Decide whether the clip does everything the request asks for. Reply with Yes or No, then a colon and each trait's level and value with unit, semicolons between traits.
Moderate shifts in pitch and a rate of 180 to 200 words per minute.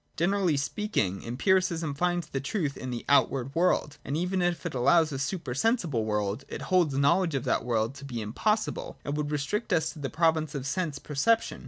Yes: average, 4.7 semitones; average, 195 wpm